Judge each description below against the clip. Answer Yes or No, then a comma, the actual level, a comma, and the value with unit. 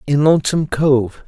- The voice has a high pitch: No, medium, 145 Hz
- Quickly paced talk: No, average, 140 wpm